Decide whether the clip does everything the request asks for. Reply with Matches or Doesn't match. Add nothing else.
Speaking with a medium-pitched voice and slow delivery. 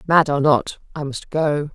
Doesn't match